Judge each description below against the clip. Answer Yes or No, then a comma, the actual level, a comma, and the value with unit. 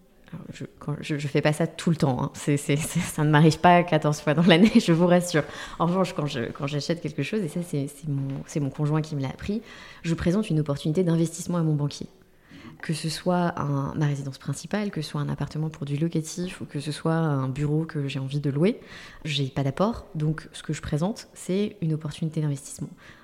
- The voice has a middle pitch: Yes, medium, 155 Hz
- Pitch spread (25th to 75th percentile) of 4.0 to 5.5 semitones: No, average, 3.0 semitones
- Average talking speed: No, fast, 230 wpm